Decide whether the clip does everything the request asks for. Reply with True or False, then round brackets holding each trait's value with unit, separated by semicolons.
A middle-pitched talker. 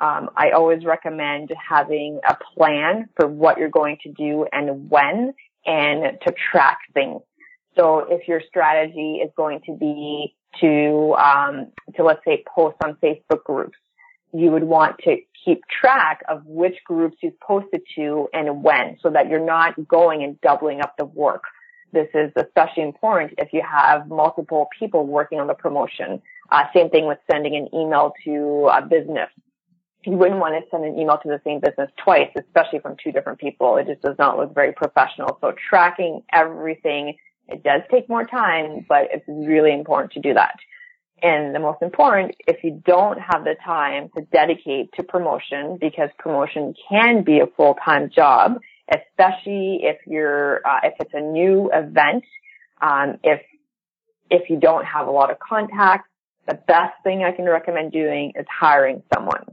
True (160 Hz)